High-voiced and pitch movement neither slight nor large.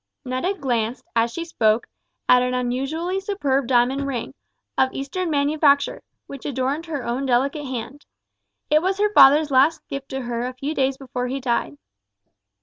Yes: very high, 270 Hz; average, 3.0 semitones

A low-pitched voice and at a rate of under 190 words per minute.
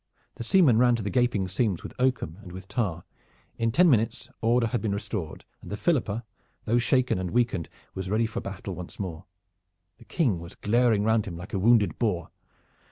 No: low, 110 Hz; average, 195 wpm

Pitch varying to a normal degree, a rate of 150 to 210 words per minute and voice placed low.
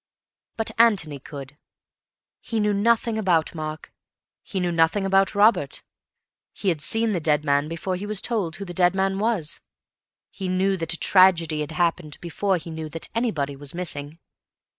No: average, 4.3 semitones; average, 170 wpm; medium, 175 Hz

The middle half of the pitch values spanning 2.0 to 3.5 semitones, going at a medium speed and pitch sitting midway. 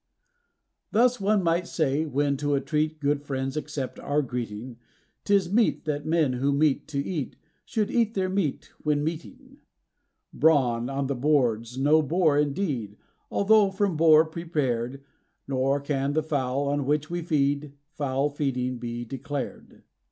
Yes: average, 3.2 semitones; average, 150 wpm; medium, 145 Hz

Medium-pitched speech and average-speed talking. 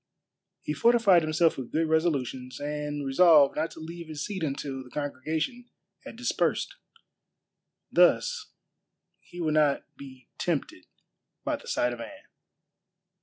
No: medium, 155 Hz; slow, 130 wpm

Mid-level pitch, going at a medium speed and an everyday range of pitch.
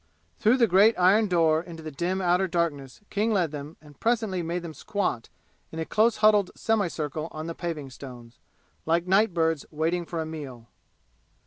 Yes: medium, 170 Hz; average, 175 wpm; average, 3.8 semitones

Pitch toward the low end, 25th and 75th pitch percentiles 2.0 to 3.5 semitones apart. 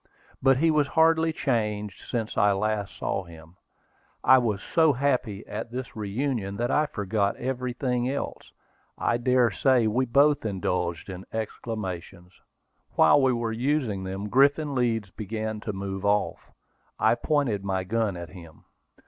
No: low, 110 Hz; average, 4.9 semitones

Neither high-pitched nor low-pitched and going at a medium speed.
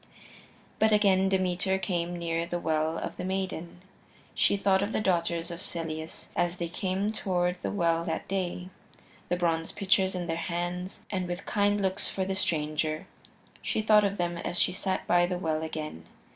Yes: medium, 180 Hz; average, 180 wpm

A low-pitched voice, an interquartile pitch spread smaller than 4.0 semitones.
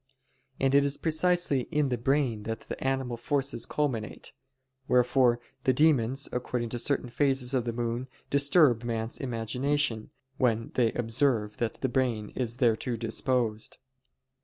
Yes: low, 125 Hz; average, 3.0 semitones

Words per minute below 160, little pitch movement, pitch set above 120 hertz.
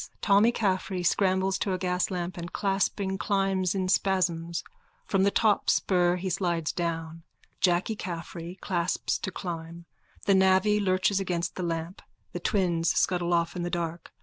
Yes: average, 150 wpm; narrow, 2.0 semitones; medium, 185 Hz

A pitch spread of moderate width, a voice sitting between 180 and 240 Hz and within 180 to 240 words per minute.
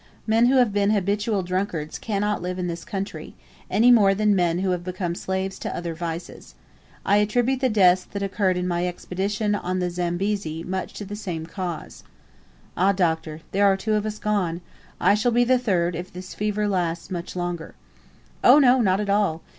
Yes: average, 3.0 semitones; high, 190 Hz; average, 195 wpm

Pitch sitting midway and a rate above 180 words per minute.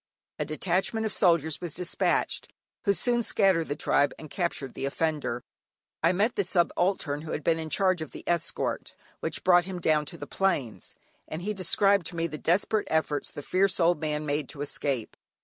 Yes: medium, 165 Hz; average, 190 wpm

